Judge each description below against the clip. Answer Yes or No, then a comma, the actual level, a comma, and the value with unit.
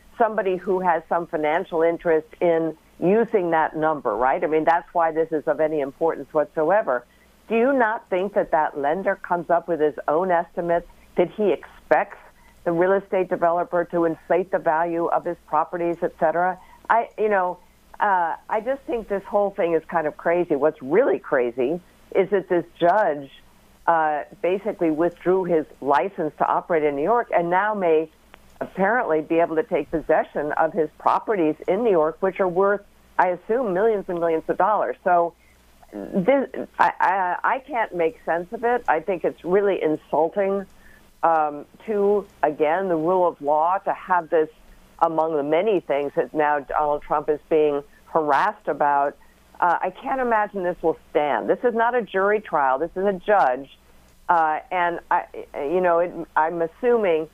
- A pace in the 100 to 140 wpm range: No, average, 175 wpm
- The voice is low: No, medium, 170 Hz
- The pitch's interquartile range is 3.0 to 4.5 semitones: Yes, average, 3.8 semitones